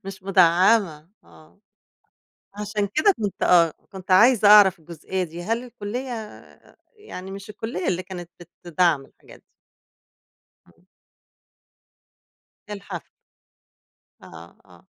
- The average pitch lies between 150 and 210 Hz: Yes, high, 190 Hz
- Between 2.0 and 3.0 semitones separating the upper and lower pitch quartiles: No, average, 3.4 semitones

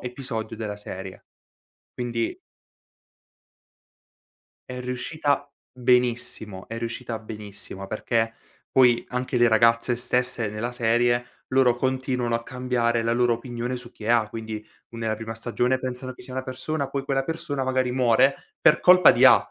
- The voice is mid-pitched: No, low, 120 Hz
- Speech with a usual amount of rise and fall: No, narrow, 2.1 semitones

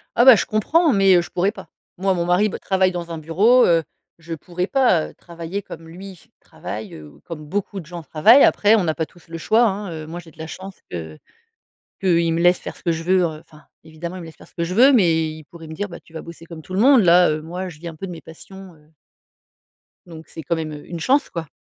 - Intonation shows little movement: No, average, 3.1 semitones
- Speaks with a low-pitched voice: No, medium, 170 Hz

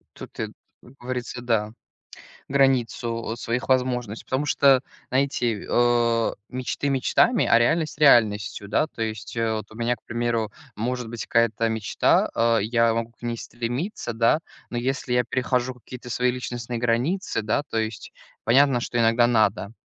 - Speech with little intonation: Yes, narrow, 1.8 semitones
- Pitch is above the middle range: No, low, 120 Hz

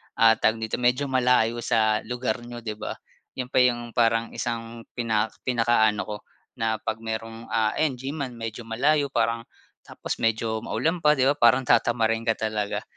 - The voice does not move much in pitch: Yes, narrow, 2.0 semitones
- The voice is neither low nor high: No, low, 115 Hz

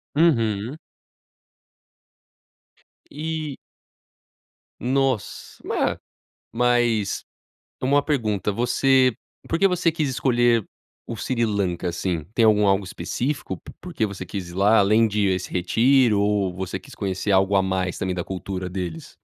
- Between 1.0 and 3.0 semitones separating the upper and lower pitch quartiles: No, average, 5.2 semitones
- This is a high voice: No, low, 105 Hz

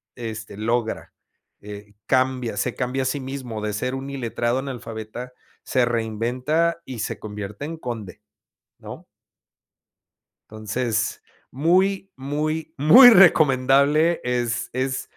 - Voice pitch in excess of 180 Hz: No, low, 125 Hz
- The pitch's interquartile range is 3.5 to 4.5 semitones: Yes, average, 4.0 semitones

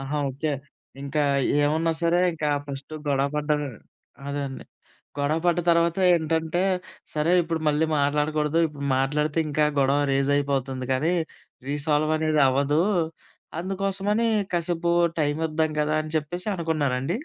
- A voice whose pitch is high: No, medium, 150 Hz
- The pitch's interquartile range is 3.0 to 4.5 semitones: No, narrow, 2.5 semitones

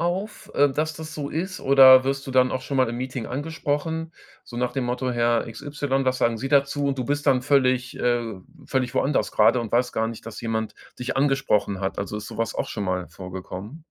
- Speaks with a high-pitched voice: No, low, 130 Hz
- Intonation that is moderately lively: Yes, average, 3.5 semitones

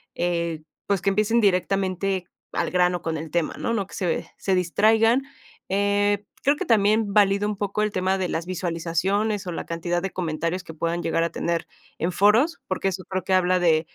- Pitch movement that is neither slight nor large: Yes, average, 3.0 semitones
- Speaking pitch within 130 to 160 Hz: No, medium, 185 Hz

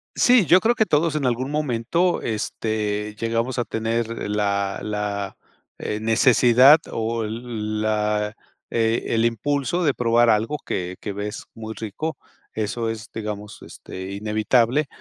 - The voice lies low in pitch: Yes, low, 115 Hz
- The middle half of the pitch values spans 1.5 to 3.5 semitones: Yes, average, 2.9 semitones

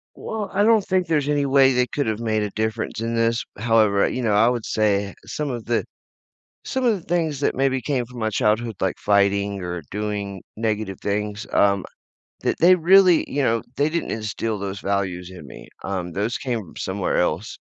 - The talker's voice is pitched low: Yes, low, 110 Hz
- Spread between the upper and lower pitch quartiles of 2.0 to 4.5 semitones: No, average, 5.3 semitones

